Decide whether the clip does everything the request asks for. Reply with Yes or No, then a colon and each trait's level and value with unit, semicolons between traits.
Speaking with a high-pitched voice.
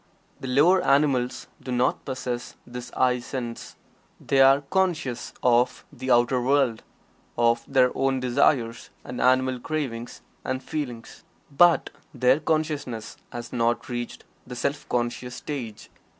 No: low, 125 Hz